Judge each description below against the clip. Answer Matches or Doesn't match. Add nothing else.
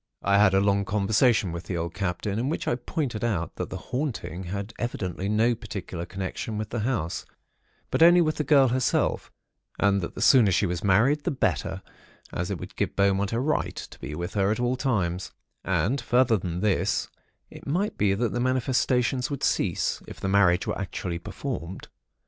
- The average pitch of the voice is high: Doesn't match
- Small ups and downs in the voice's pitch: Doesn't match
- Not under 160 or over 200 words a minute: Matches